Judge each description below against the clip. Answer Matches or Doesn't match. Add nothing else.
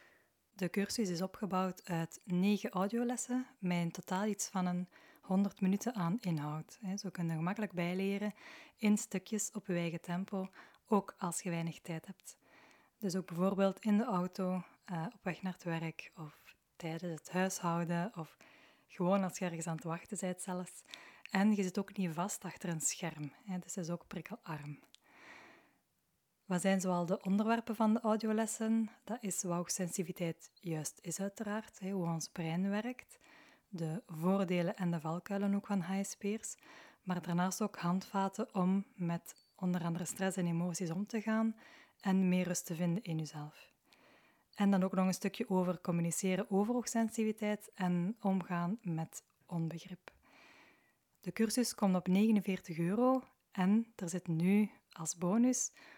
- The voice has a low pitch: Doesn't match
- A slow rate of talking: Doesn't match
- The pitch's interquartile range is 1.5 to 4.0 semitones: Matches